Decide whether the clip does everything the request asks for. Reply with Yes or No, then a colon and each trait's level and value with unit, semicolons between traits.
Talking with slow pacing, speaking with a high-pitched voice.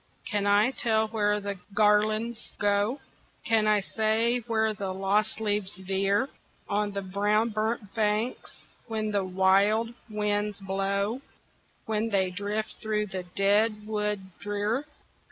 Yes: slow, 130 wpm; high, 210 Hz